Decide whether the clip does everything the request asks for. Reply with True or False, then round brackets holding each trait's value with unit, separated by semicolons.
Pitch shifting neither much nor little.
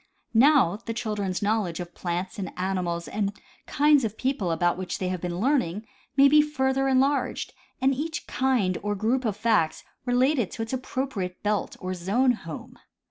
False (6.2 semitones)